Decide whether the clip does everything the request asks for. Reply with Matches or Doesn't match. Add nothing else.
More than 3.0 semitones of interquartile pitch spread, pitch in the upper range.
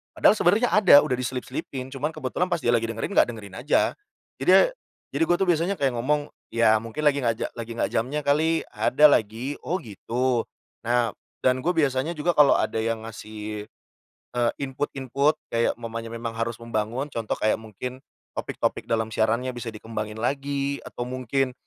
Doesn't match